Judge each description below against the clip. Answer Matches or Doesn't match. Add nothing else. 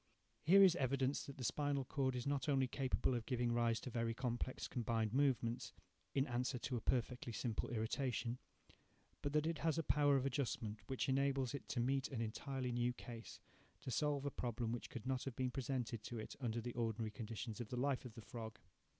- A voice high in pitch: Doesn't match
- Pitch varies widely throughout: Doesn't match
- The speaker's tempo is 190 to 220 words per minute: Matches